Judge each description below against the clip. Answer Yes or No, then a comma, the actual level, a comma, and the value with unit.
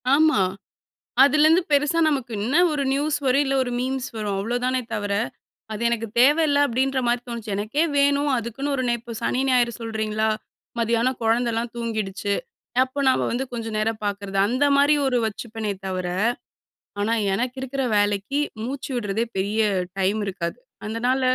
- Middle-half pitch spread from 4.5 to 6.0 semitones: No, average, 3.8 semitones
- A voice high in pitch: Yes, high, 235 Hz